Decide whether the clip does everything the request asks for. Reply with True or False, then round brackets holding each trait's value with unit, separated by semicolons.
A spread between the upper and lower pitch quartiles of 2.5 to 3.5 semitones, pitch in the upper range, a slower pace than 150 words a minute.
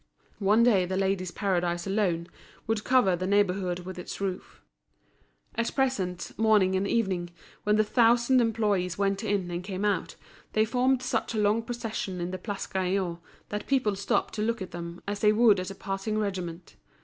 False (3.1 semitones; 200 Hz; 180 wpm)